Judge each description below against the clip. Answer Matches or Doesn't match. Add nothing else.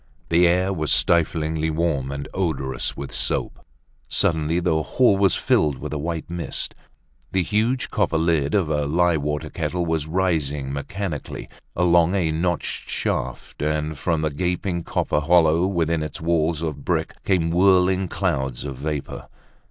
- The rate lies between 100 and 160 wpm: Matches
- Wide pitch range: Doesn't match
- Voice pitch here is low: Matches